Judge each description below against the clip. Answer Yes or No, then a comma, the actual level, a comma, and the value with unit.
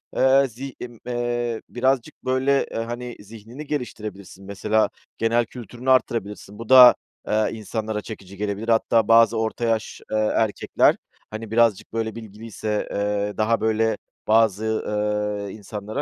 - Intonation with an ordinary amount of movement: No, narrow, 2.3 semitones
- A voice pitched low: Yes, low, 110 Hz